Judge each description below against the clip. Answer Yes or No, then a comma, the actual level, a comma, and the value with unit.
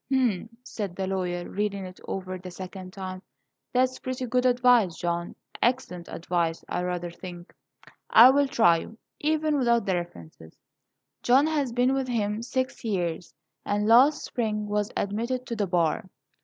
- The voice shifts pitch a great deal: Yes, wide, 5.7 semitones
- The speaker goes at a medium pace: Yes, average, 155 wpm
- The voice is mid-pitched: No, high, 210 Hz